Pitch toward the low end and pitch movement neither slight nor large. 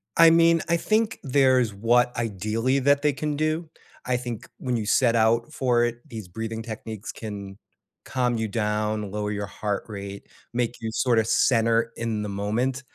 Yes: low, 115 Hz; average, 3.4 semitones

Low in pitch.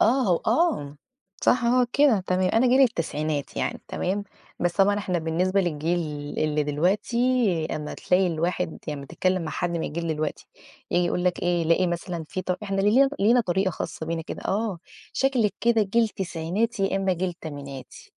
No: medium, 185 Hz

